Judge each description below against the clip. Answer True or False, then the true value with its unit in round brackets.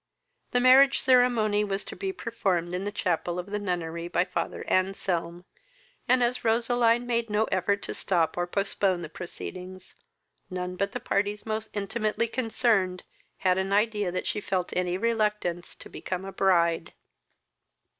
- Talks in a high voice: True (200 Hz)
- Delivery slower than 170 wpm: True (155 wpm)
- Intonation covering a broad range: False (3.7 semitones)